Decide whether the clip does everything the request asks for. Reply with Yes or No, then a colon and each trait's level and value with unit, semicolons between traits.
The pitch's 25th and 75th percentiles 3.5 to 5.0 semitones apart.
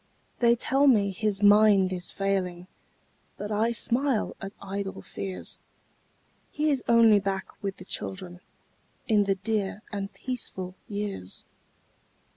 No: average, 2.7 semitones